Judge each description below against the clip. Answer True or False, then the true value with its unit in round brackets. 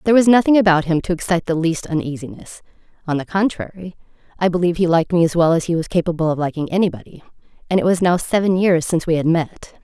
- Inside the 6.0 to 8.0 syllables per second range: True (7.0 syllables/s)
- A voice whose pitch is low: False (175 Hz)